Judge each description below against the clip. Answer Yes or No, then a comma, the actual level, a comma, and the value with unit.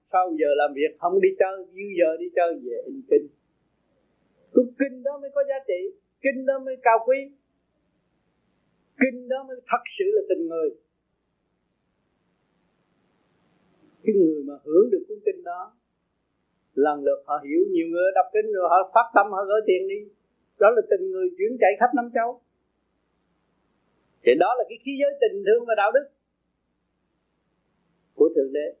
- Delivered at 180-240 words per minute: No, average, 170 wpm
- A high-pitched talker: Yes, very high, 270 Hz